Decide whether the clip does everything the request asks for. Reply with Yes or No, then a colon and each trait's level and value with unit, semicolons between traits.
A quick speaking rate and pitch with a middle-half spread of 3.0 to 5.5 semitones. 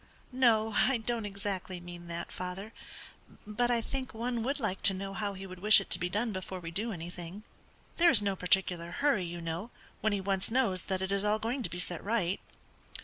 Yes: fast, 215 wpm; average, 3.7 semitones